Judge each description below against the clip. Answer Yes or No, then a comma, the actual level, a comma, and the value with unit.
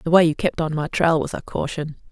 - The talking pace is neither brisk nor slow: No, fast, 285 wpm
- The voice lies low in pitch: No, medium, 160 Hz